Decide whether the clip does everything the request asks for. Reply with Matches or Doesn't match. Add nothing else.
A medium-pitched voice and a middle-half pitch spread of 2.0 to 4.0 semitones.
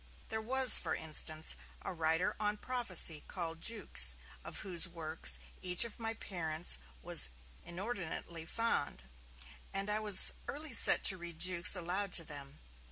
Doesn't match